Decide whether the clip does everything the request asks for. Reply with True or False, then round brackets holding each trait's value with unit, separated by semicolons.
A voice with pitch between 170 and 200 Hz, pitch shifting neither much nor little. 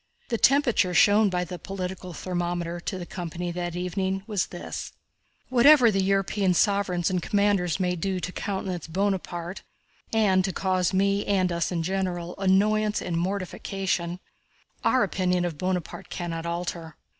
False (185 Hz; 2.0 semitones)